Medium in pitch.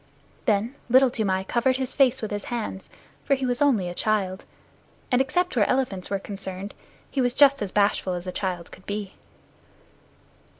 No: high, 215 Hz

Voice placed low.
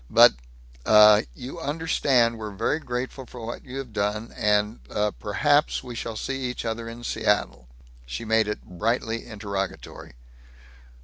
Yes: low, 115 Hz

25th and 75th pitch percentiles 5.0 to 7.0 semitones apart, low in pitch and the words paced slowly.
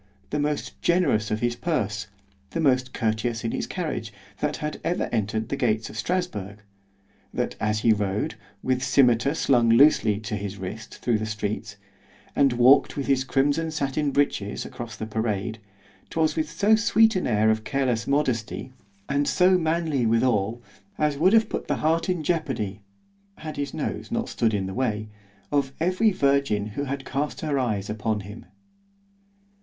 No: wide, 5.5 semitones; low, 120 Hz; average, 160 wpm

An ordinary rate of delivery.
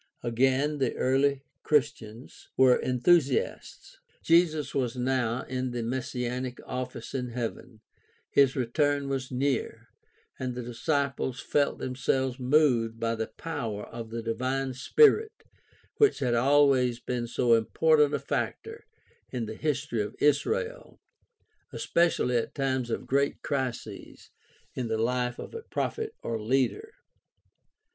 No: slow, 130 wpm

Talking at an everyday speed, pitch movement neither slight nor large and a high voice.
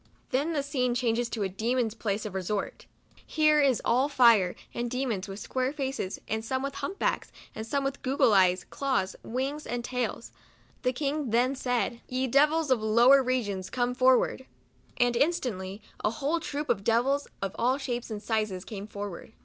Yes: average, 185 wpm; average, 3.9 semitones; high, 245 Hz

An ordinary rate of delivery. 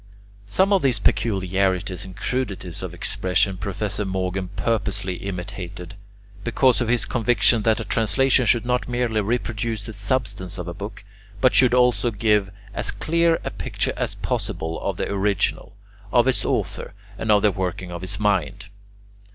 Yes: average, 160 wpm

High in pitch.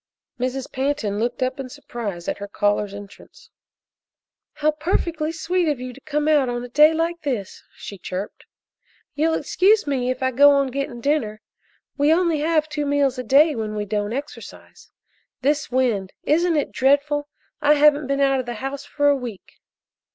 Yes: very high, 275 Hz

